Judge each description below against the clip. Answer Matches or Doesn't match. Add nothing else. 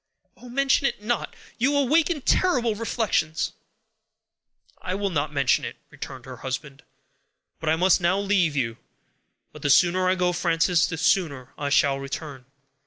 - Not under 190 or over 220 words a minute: Doesn't match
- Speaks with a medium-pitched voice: Matches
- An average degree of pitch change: Doesn't match